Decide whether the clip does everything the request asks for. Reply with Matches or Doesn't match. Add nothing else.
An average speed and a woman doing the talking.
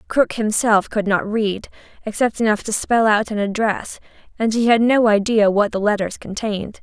Matches